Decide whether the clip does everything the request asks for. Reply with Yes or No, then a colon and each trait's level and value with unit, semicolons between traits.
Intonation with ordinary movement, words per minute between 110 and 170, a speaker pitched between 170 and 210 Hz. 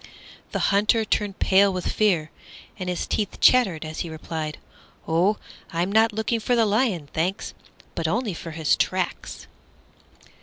Yes: average, 4.7 semitones; average, 150 wpm; high, 190 Hz